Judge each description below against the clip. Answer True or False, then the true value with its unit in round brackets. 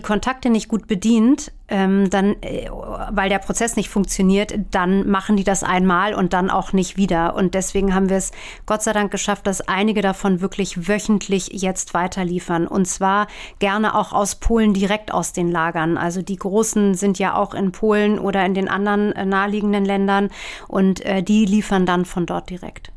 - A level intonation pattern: True (1.8 semitones)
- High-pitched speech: True (195 Hz)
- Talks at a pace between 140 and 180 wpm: True (175 wpm)